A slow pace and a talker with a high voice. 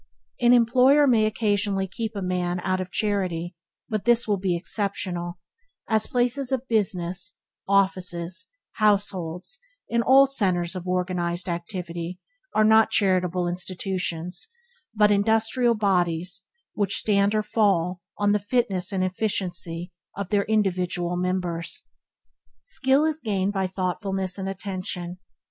Yes: slow, 130 wpm; high, 195 Hz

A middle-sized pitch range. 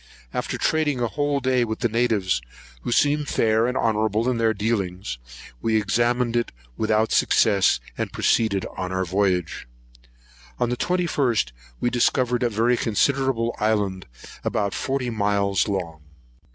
Yes: average, 3.4 semitones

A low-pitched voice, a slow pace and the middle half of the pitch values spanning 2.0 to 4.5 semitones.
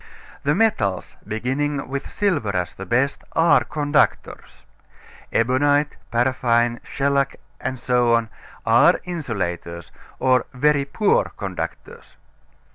Yes: low, 130 Hz; slow, 95 wpm; average, 3.9 semitones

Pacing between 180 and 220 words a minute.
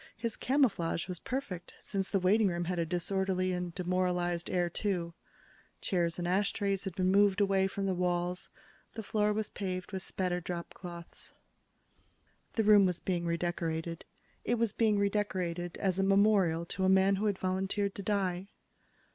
No: average, 165 wpm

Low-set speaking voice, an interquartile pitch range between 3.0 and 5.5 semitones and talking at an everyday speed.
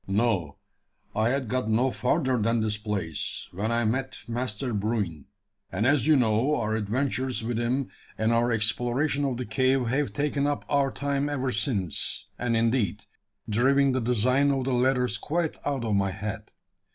Yes: low, 120 Hz; average, 3.7 semitones; average, 170 wpm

